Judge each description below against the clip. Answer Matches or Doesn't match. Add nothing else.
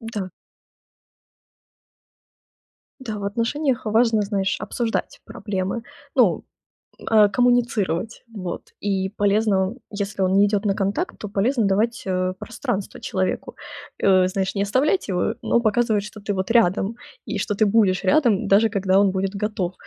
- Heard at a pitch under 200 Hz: Doesn't match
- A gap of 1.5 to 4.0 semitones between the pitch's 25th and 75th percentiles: Matches